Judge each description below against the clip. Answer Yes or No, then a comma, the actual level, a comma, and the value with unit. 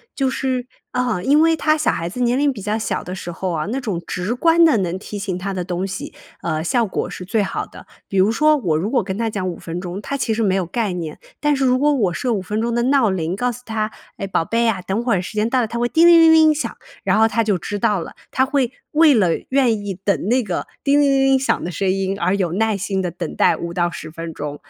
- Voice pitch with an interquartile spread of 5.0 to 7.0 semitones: Yes, wide, 5.6 semitones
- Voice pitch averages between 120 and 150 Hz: No, high, 215 Hz